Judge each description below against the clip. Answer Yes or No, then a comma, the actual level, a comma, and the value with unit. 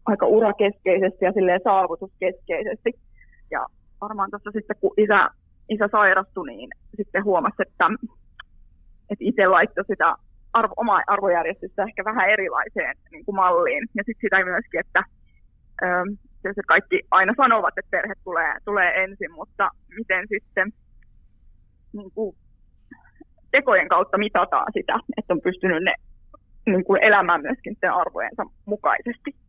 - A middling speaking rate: Yes, average, 130 wpm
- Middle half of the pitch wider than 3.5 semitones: No, narrow, 2.6 semitones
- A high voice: Yes, high, 200 Hz